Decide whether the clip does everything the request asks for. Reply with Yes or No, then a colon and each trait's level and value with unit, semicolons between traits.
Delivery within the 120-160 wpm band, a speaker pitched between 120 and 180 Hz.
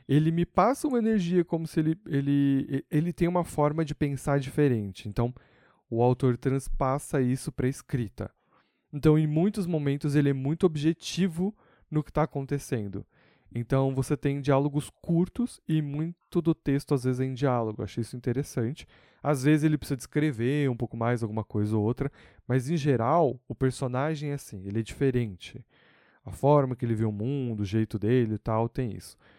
No: fast, 185 wpm; medium, 140 Hz